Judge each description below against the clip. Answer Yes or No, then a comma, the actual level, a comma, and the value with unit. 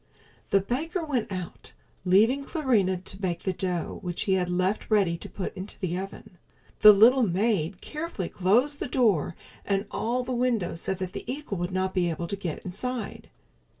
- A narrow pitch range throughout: No, average, 5.0 semitones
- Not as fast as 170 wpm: No, average, 185 wpm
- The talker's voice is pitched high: Yes, high, 195 Hz